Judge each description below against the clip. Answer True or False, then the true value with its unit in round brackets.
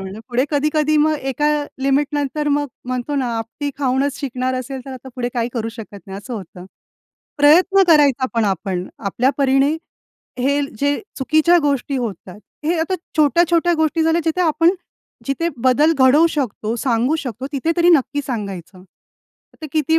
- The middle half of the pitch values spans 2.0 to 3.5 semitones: False (4.1 semitones)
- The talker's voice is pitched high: True (275 Hz)